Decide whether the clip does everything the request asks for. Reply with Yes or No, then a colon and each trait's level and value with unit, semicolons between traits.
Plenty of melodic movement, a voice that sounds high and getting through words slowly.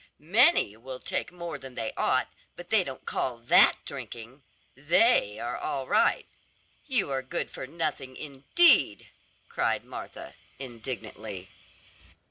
No: wide, 6.4 semitones; low, 135 Hz; slow, 125 wpm